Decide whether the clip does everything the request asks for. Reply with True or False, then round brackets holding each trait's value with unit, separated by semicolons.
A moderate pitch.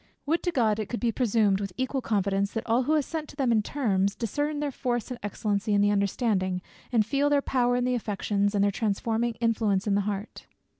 False (225 Hz)